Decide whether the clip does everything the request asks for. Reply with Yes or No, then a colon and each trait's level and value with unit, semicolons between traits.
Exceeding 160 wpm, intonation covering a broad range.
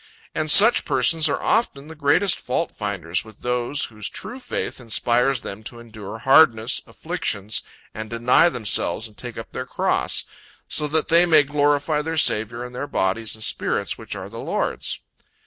Yes: average, 170 wpm; wide, 5.8 semitones